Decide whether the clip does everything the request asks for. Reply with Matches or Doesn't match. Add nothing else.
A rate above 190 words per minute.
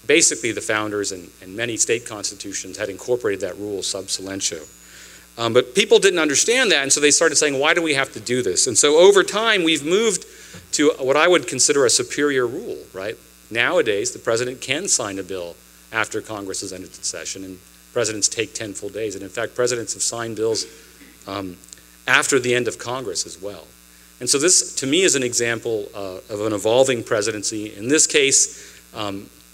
Matches